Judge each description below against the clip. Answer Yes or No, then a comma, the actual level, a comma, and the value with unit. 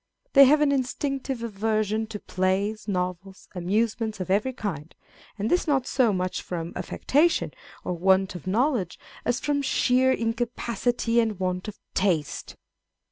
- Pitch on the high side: Yes, high, 215 Hz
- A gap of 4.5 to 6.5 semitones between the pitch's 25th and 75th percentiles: Yes, average, 5.0 semitones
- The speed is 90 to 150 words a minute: Yes, average, 140 wpm